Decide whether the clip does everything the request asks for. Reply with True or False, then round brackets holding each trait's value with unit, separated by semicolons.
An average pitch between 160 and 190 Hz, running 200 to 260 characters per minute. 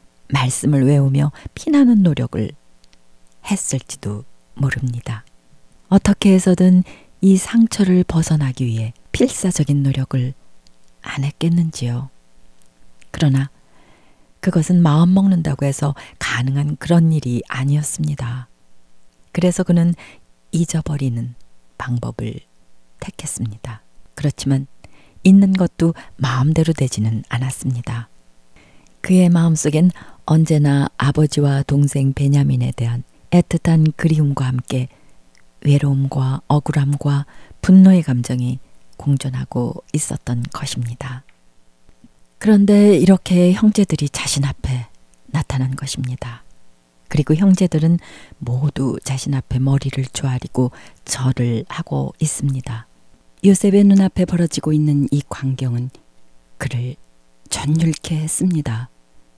False (135 Hz; 245 characters per minute)